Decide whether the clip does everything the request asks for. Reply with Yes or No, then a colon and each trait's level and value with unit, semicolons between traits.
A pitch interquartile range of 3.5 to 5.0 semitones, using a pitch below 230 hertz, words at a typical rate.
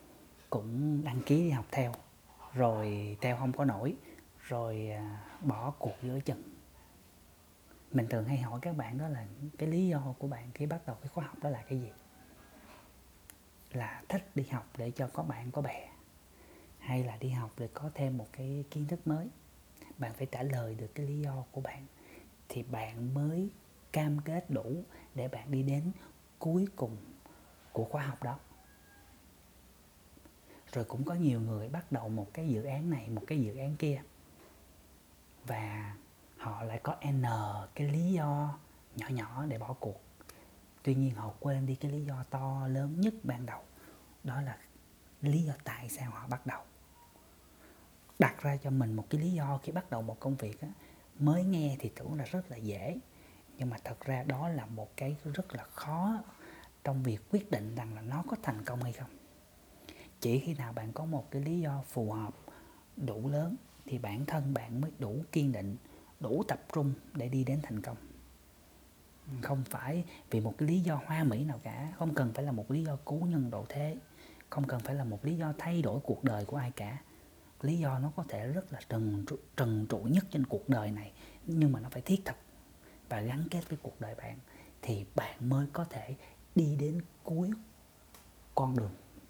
Yes: average, 4.7 semitones; low, 135 Hz; average, 195 wpm